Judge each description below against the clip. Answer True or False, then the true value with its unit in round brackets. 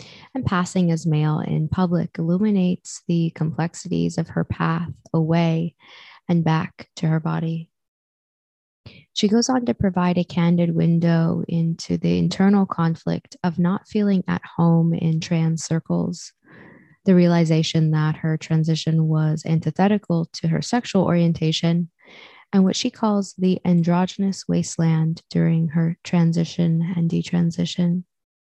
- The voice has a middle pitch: True (170 Hz)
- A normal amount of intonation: False (1.8 semitones)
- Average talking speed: False (130 wpm)